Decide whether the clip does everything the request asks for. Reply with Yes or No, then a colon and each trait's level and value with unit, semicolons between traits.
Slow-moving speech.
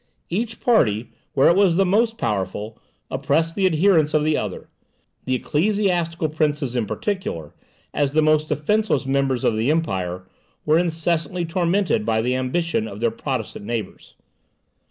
No: average, 150 wpm